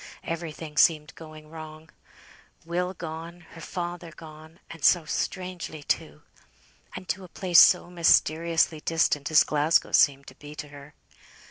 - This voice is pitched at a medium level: Yes, medium, 160 Hz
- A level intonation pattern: Yes, narrow, 2.0 semitones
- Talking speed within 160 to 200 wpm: No, average, 140 wpm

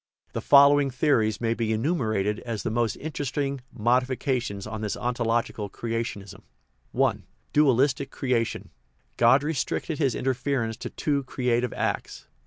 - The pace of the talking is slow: Yes, slow, 125 wpm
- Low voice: Yes, low, 120 Hz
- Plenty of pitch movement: No, average, 3.5 semitones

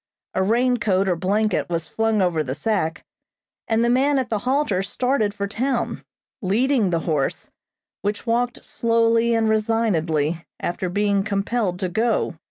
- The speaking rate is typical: Yes, average, 155 wpm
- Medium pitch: No, high, 210 Hz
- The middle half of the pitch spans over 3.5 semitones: Yes, average, 4.0 semitones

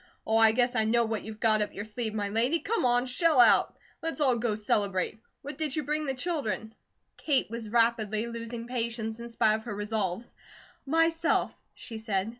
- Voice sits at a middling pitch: No, high, 230 Hz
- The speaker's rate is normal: Yes, average, 195 wpm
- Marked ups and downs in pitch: No, average, 2.8 semitones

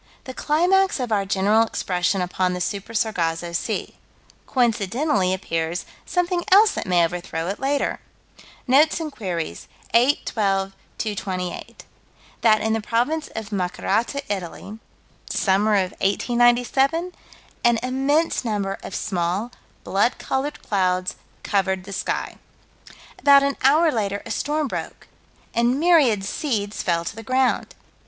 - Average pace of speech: No, slow, 130 wpm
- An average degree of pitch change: No, wide, 6.1 semitones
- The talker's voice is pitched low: No, high, 215 Hz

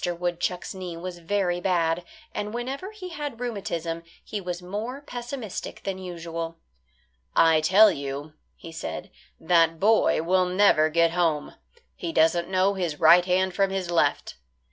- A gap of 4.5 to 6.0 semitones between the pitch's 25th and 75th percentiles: No, average, 3.4 semitones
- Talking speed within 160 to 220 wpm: No, average, 145 wpm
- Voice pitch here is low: No, medium, 180 Hz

